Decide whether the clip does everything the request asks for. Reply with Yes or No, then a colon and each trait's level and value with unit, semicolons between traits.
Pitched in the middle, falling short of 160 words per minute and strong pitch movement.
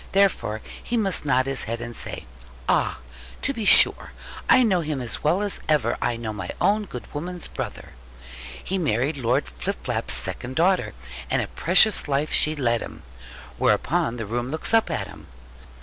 No: medium, 145 Hz; average, 175 wpm; wide, 7.6 semitones